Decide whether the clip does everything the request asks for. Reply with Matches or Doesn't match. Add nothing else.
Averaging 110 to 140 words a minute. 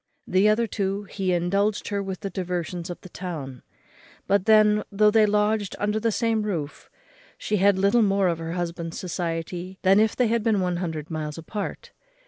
Doesn't match